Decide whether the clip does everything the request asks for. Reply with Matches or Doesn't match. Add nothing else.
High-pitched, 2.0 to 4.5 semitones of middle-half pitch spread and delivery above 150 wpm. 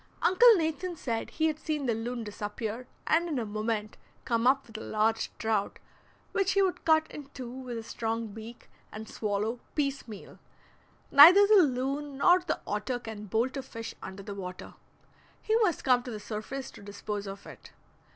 Doesn't match